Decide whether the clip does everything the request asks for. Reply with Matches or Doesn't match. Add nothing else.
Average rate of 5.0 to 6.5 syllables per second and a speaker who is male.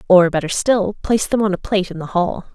Doesn't match